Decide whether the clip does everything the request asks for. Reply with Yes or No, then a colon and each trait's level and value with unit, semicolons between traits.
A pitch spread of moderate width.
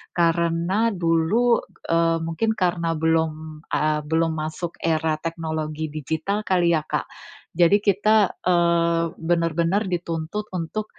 No: narrow, 2.0 semitones